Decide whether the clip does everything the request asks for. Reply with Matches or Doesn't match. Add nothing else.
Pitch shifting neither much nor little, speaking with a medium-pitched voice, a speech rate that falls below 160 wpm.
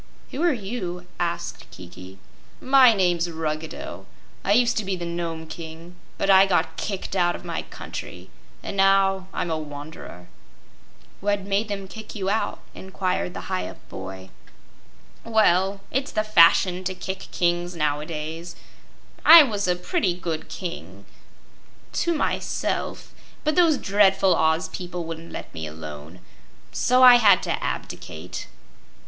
Matches